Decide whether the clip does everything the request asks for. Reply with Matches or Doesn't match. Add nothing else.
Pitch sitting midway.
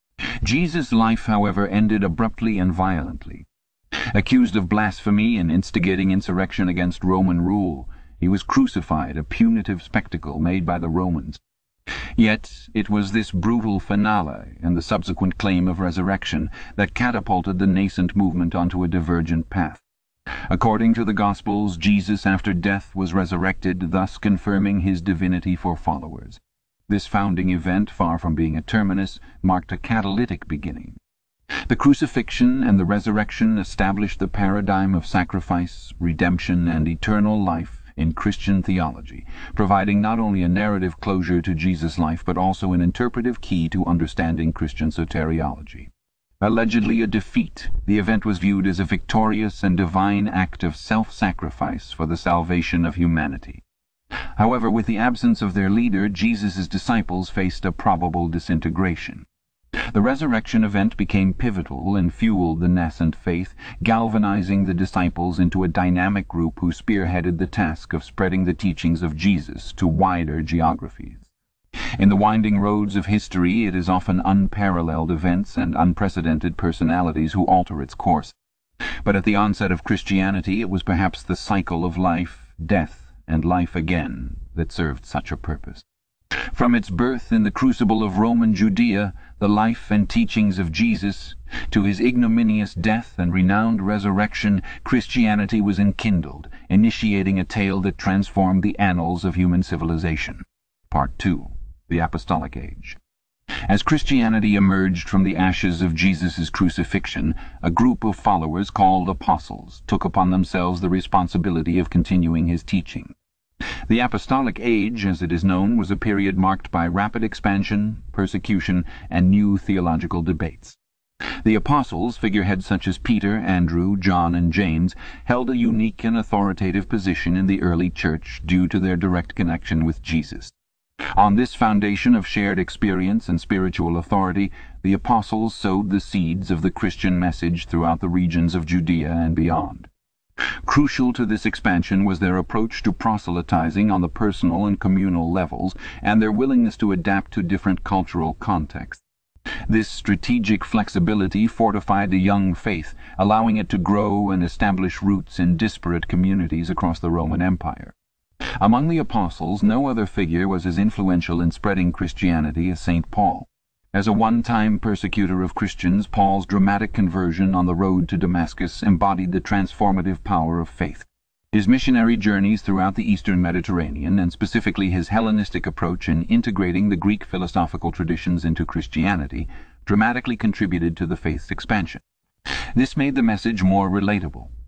Doesn't match